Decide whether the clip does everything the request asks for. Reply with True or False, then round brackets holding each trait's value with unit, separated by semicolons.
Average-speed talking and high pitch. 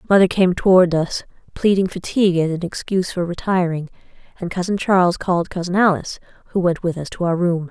False (185 wpm; 180 Hz)